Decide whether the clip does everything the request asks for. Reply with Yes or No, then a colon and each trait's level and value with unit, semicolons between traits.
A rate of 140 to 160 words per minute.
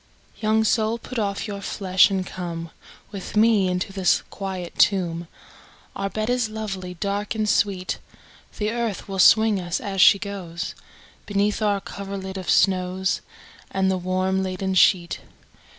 Yes: average, 150 wpm